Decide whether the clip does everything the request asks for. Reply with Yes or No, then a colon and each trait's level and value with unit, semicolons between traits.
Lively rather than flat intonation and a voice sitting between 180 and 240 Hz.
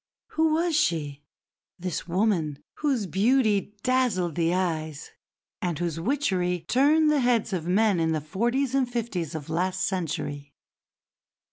Yes: wide, 6.9 semitones; medium, 185 Hz